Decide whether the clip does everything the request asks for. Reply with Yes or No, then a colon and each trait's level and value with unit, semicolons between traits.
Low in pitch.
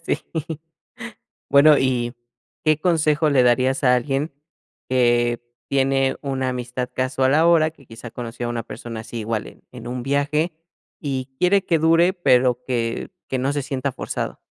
Yes: low, 130 Hz